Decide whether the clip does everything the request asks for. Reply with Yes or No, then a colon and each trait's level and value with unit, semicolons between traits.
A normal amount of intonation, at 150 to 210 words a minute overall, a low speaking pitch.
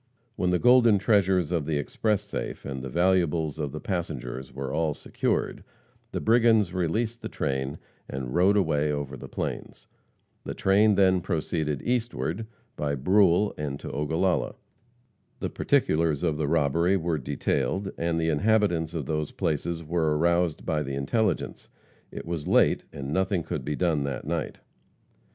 Yes: average, 4.4 semitones; average, 155 wpm; very low, 85 Hz